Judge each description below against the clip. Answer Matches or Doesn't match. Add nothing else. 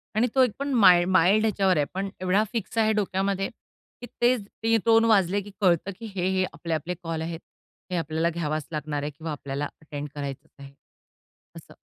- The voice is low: Doesn't match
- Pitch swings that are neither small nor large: Matches